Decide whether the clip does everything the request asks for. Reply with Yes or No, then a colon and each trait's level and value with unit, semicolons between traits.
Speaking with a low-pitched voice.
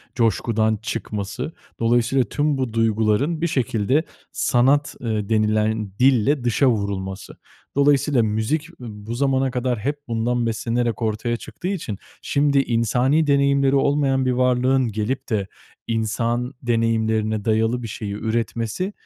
Yes: low, 120 Hz